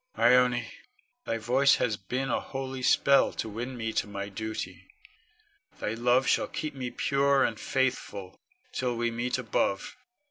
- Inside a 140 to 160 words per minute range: Yes, average, 150 wpm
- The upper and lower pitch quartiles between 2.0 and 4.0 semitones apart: Yes, average, 2.9 semitones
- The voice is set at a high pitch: No, low, 125 Hz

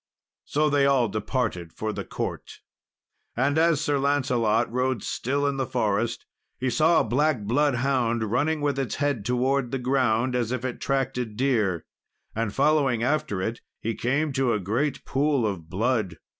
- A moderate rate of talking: Yes, average, 170 wpm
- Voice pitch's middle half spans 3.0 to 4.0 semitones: Yes, average, 3.7 semitones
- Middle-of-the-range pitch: No, low, 125 Hz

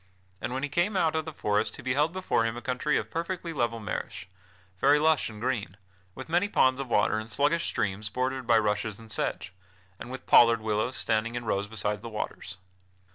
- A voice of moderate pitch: No, low, 120 Hz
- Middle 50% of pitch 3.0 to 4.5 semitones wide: No, average, 5.2 semitones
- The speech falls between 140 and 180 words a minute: No, fast, 205 wpm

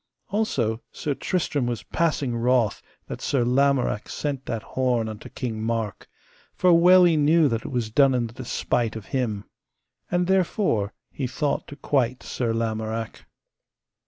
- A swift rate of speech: No, average, 155 wpm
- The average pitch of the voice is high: No, low, 125 Hz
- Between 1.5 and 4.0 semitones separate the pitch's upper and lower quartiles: No, average, 4.4 semitones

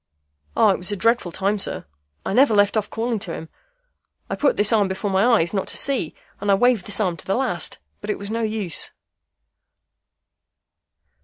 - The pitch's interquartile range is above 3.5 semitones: No, average, 3.0 semitones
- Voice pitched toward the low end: No, high, 205 Hz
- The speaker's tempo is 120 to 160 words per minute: No, average, 200 wpm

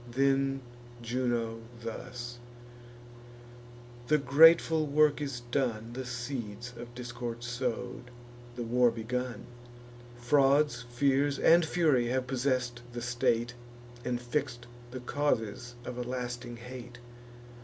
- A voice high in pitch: No, low, 125 Hz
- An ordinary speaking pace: No, slow, 110 wpm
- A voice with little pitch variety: Yes, narrow, 2.1 semitones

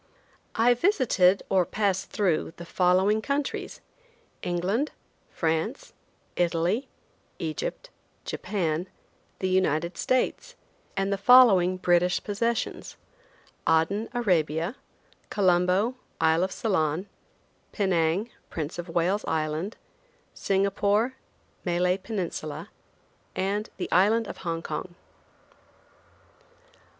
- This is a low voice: No, high, 190 Hz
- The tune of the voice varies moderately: Yes, average, 3.9 semitones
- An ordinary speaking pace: No, slow, 90 wpm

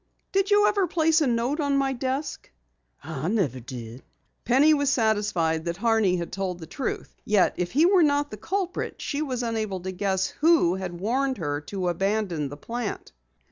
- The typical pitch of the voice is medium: No, high, 220 Hz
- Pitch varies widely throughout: Yes, wide, 8.1 semitones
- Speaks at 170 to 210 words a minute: Yes, average, 180 wpm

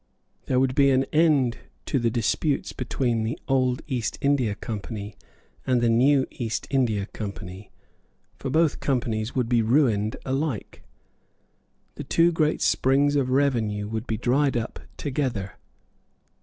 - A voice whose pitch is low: Yes, low, 125 Hz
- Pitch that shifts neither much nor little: Yes, average, 3.7 semitones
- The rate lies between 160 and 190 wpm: No, average, 140 wpm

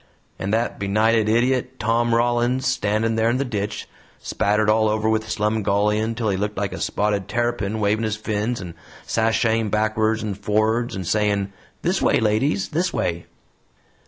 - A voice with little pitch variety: Yes, narrow, 1.8 semitones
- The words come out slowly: No, average, 160 wpm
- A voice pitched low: Yes, low, 110 Hz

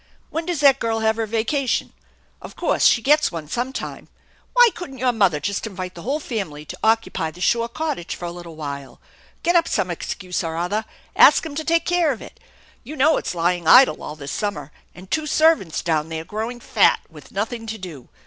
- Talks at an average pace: No, fast, 210 wpm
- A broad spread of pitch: Yes, wide, 8.1 semitones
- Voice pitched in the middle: No, high, 220 Hz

